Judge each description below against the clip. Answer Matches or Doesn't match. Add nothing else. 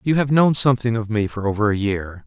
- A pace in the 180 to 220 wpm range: Doesn't match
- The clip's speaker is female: Doesn't match